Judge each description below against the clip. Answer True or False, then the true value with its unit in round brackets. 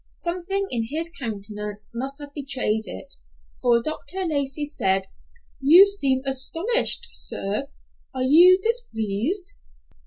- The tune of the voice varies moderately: False (7.2 semitones)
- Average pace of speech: False (115 wpm)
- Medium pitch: False (275 Hz)